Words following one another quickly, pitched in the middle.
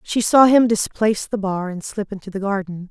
No: fast, 225 wpm; high, 205 Hz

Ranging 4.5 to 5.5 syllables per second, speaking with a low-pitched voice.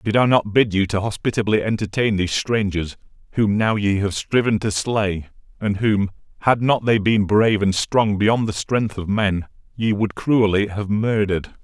Yes: 4.7 syllables/s; low, 105 Hz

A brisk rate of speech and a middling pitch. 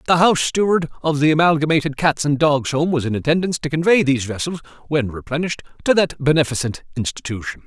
No: average, 170 wpm; medium, 150 Hz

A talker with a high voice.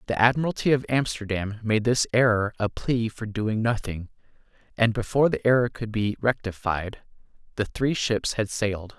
No: low, 110 Hz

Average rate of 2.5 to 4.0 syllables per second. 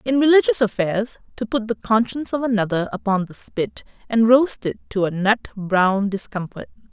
No: 5.1 syllables/s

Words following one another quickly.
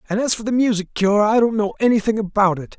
Yes: fast, 260 wpm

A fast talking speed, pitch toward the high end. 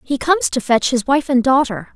Yes: fast, 245 wpm; very high, 260 Hz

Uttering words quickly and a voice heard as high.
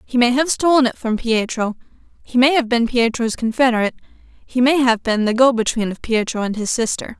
Yes: fast, 210 wpm; high, 240 Hz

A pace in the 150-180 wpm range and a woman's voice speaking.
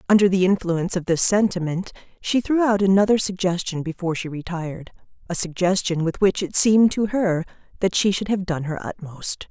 Yes: average, 175 wpm; female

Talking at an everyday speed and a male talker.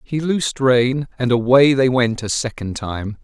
Yes: average, 185 wpm; male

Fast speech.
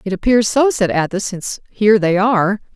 No: average, 195 wpm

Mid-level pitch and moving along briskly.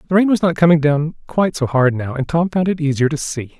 Yes: medium, 155 Hz; fast, 285 wpm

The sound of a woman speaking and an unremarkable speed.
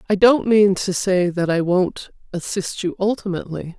Yes: female; average, 175 wpm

